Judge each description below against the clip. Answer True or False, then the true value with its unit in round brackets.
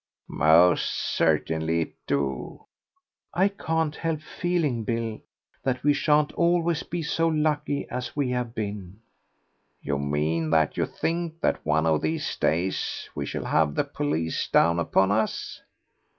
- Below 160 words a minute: True (140 wpm)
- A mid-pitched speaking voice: False (110 Hz)